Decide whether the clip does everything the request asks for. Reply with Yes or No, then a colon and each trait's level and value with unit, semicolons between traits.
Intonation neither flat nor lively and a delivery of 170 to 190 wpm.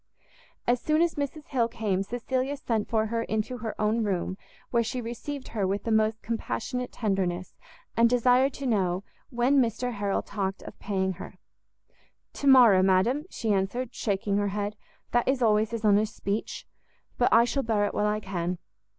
Yes: average, 3.5 semitones; average, 175 wpm